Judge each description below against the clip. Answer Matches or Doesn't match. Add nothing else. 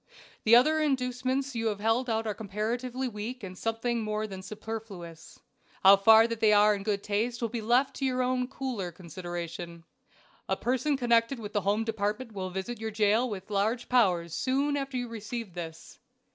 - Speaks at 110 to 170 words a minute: Doesn't match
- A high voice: Matches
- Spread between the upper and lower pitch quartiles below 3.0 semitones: Doesn't match